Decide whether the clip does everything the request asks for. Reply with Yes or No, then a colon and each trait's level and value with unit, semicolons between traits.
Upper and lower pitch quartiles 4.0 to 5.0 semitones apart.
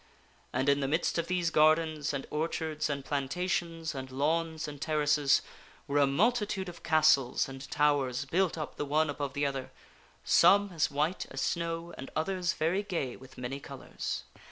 No: average, 3.2 semitones